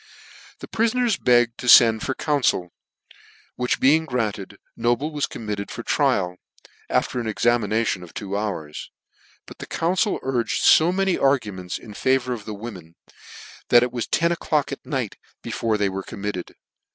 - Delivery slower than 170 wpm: Yes, average, 160 wpm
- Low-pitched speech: Yes, low, 120 Hz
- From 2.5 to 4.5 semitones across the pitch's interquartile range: No, average, 5.1 semitones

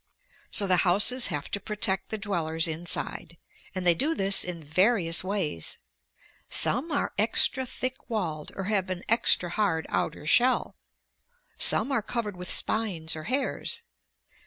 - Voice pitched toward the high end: Yes, high, 195 Hz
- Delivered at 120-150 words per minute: Yes, average, 145 wpm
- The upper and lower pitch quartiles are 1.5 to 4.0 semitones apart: No, average, 5.0 semitones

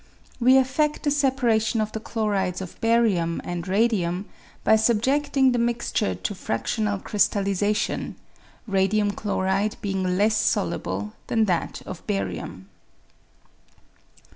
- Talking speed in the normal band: No, slow, 115 wpm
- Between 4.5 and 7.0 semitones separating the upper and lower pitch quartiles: No, average, 3.7 semitones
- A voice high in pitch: Yes, high, 210 Hz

